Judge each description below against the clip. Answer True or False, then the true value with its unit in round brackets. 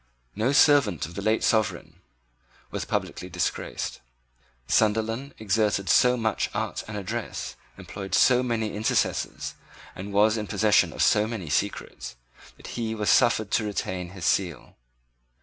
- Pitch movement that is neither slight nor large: False (2.2 semitones)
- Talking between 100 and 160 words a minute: True (140 wpm)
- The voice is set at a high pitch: False (105 Hz)